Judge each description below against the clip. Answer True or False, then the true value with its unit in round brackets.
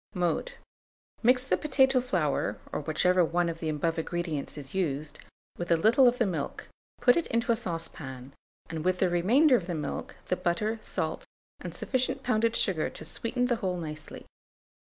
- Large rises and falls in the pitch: True (6.6 semitones)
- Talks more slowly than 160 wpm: False (175 wpm)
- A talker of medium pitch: True (180 Hz)